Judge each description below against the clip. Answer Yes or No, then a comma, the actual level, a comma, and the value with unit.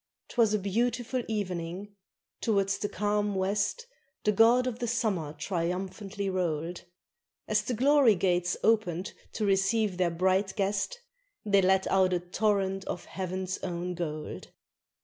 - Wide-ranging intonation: No, average, 3.0 semitones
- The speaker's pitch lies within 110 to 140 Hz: No, high, 195 Hz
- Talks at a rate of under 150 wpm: Yes, average, 140 wpm